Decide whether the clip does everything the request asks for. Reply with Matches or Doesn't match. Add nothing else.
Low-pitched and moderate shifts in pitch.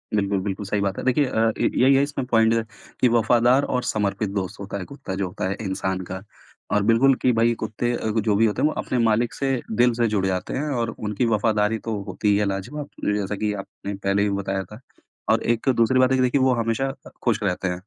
Matches